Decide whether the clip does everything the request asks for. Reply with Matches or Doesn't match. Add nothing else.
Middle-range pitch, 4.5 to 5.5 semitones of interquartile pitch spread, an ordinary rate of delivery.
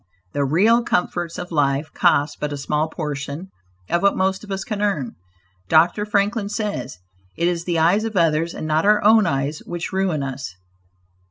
Matches